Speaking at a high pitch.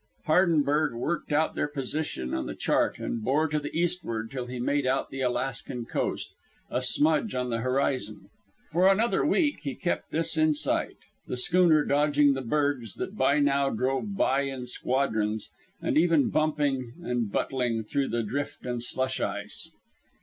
No: medium, 140 Hz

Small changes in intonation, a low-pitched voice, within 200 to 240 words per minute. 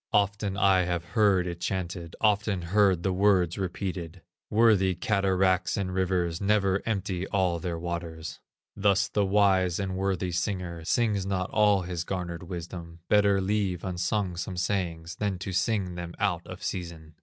No: narrow, 2.2 semitones; very low, 95 Hz; average, 155 wpm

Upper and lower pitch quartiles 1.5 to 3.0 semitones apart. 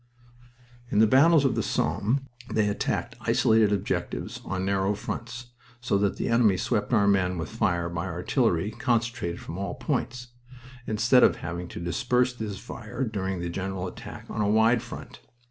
No: average, 4.1 semitones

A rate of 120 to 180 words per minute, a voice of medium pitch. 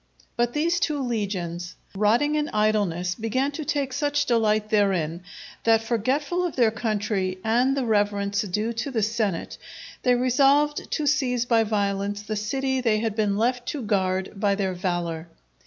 No: average, 160 wpm; high, 220 Hz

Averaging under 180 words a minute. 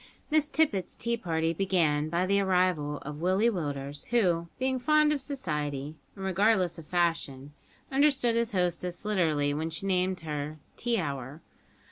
Yes: average, 150 wpm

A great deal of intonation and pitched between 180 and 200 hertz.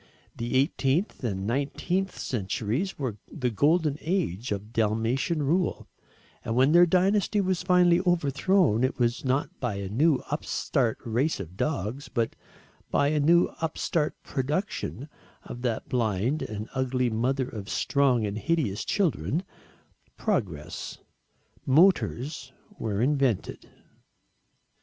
No: wide, 6.2 semitones; low, 135 Hz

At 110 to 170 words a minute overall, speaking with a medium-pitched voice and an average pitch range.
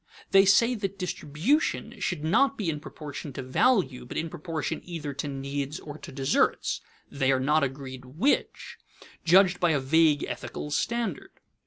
Yes: average, 160 wpm; medium, 155 Hz; average, 5.0 semitones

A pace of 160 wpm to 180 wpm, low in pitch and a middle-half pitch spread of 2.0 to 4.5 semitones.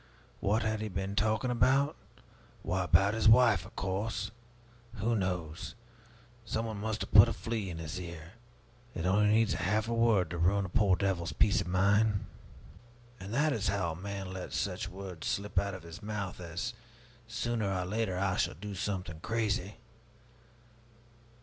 Yes: average, 170 wpm; low, 100 Hz; average, 3.0 semitones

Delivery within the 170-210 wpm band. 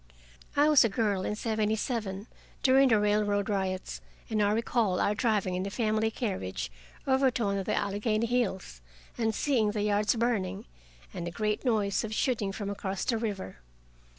Yes: average, 180 wpm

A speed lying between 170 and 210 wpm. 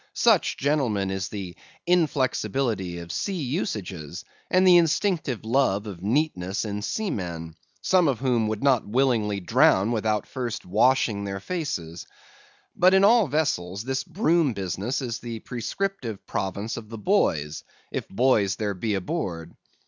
No: average, 140 wpm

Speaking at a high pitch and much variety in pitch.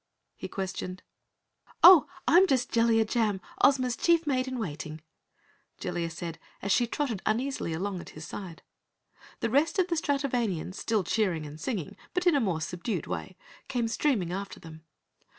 Yes: high, 220 Hz; wide, 6.8 semitones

